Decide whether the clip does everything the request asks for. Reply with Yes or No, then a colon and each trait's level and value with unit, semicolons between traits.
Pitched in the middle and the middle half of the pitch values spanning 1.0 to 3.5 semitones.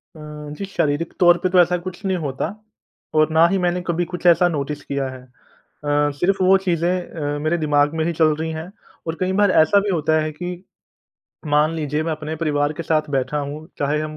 Yes: medium, 160 Hz; average, 2.9 semitones